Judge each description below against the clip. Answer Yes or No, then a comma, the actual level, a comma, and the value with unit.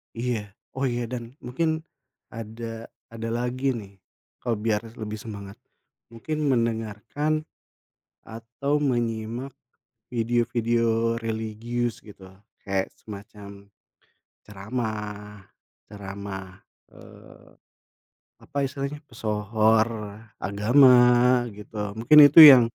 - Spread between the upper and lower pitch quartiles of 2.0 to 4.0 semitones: Yes, average, 2.8 semitones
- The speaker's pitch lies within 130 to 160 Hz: No, low, 115 Hz